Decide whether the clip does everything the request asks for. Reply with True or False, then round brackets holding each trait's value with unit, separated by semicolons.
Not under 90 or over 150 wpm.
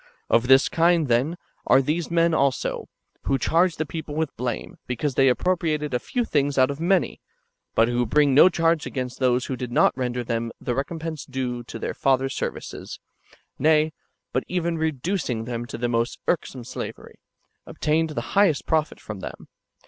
False (175 wpm)